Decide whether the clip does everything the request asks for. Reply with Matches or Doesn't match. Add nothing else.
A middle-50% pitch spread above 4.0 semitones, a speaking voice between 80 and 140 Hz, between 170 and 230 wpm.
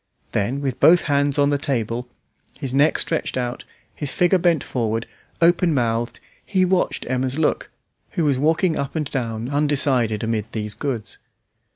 Doesn't match